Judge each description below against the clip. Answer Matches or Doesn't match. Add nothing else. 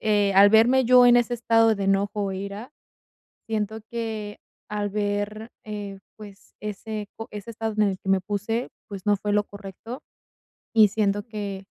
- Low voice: Doesn't match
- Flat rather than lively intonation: Matches